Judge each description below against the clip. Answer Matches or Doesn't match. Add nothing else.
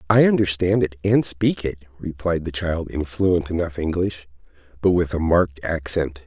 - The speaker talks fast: Doesn't match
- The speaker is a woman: Doesn't match